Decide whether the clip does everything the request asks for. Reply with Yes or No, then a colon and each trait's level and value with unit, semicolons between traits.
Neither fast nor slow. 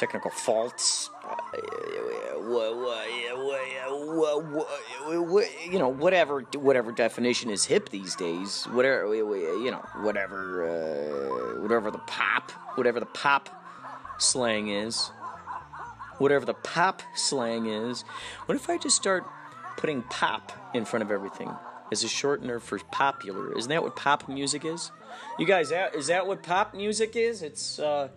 Yes: average, 150 wpm